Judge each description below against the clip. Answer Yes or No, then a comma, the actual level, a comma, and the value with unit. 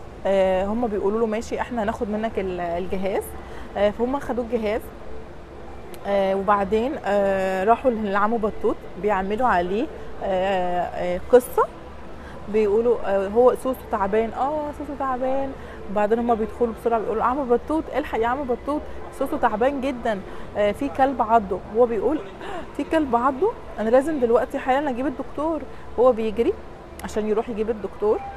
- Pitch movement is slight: No, average, 4.8 semitones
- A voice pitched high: Yes, high, 235 Hz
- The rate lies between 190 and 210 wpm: No, average, 140 wpm